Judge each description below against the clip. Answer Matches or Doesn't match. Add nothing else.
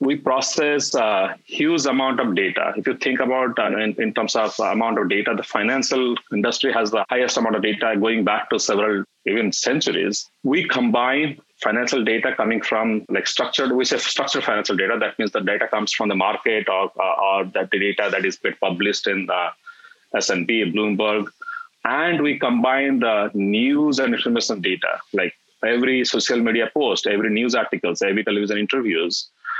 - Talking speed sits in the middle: Matches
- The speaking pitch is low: Matches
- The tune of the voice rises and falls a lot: Matches